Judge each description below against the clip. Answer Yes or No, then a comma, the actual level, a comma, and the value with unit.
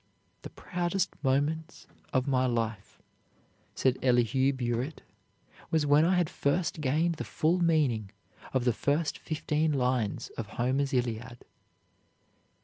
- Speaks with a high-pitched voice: No, low, 135 Hz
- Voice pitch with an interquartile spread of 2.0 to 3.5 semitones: No, average, 4.4 semitones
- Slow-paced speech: Yes, slow, 125 wpm